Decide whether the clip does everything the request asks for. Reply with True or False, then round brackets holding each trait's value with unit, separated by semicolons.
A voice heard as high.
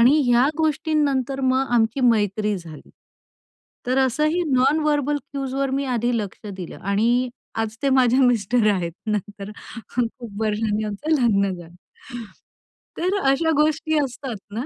True (245 Hz)